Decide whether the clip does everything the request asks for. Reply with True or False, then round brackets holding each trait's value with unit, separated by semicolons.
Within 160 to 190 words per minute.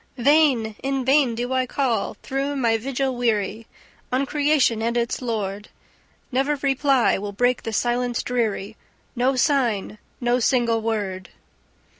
False (135 wpm)